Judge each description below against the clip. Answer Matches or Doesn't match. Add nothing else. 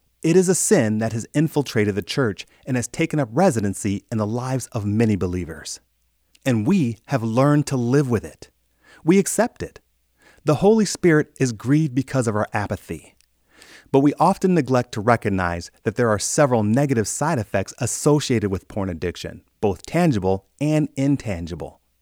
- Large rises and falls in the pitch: Matches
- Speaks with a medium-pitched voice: Doesn't match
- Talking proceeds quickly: Doesn't match